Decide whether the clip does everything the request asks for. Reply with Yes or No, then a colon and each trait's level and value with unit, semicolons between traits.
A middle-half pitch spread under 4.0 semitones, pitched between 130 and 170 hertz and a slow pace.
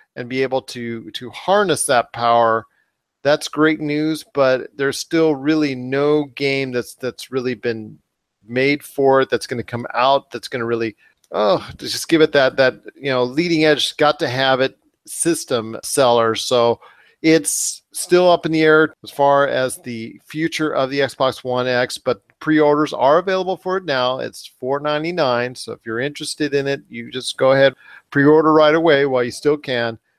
No: average, 3.6 semitones; low, 135 Hz; average, 180 wpm